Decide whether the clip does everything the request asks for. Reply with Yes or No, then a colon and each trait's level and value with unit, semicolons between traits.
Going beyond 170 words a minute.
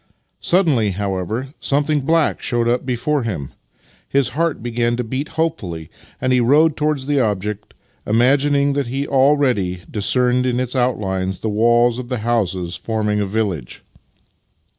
No: average, 150 wpm